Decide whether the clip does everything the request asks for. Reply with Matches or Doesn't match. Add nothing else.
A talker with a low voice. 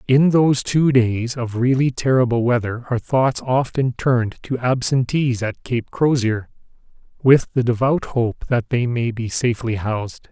Matches